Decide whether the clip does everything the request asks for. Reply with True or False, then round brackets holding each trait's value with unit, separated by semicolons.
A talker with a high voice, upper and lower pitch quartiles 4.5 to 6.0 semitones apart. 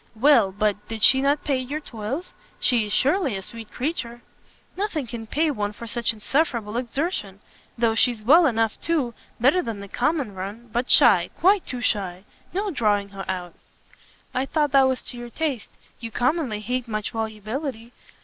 True (240 Hz; 4.8 semitones)